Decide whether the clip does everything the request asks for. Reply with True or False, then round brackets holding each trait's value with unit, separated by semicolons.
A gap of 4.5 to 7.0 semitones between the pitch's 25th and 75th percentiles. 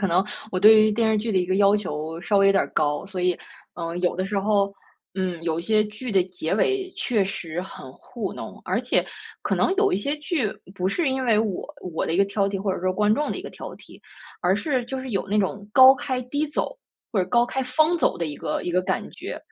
True (4.8 semitones)